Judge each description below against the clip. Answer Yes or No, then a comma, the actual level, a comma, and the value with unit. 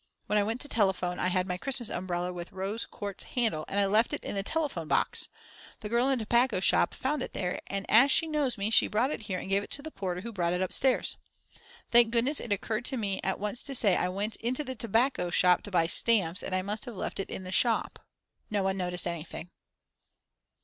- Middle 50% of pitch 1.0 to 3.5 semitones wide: No, average, 4.5 semitones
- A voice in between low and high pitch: No, high, 205 Hz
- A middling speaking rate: No, fast, 245 wpm